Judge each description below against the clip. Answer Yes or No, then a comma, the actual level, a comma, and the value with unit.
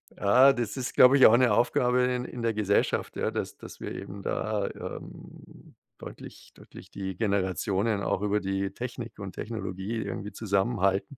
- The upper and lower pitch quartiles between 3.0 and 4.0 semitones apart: Yes, average, 3.7 semitones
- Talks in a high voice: No, low, 105 Hz